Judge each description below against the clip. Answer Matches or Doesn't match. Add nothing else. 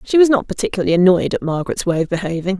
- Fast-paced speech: Matches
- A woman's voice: Matches